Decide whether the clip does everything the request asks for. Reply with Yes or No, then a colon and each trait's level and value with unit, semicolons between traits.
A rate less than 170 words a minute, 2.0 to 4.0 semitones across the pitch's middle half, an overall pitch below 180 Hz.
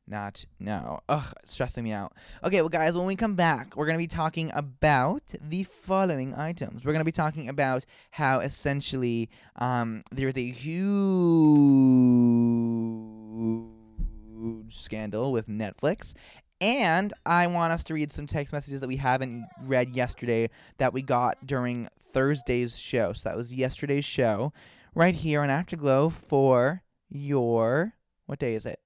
No: average, 150 wpm; average, 5.1 semitones; low, 135 Hz